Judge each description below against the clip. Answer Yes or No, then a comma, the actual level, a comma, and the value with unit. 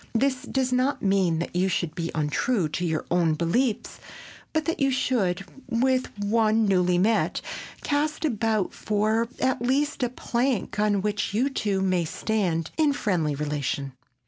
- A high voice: Yes, high, 210 Hz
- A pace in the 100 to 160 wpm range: Yes, average, 155 wpm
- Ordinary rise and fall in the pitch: No, wide, 6.3 semitones